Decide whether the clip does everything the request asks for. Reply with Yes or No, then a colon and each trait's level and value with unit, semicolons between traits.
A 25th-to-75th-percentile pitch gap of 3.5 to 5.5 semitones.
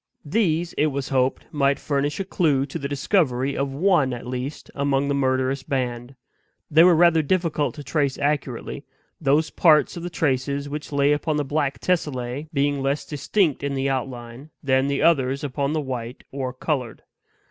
No: narrow, 2.4 semitones